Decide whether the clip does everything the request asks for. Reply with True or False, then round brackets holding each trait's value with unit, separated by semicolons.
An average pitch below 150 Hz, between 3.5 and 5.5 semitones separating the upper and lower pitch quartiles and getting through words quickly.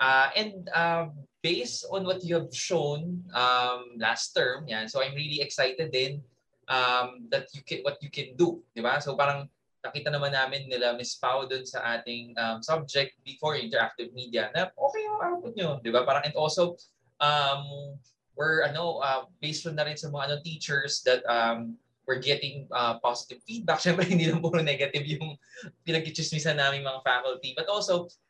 True (140 Hz; 4.1 semitones; 180 wpm)